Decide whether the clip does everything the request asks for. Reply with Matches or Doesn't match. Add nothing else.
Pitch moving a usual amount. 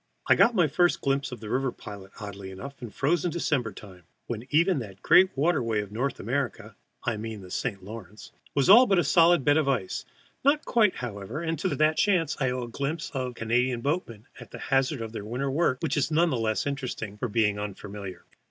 Doesn't match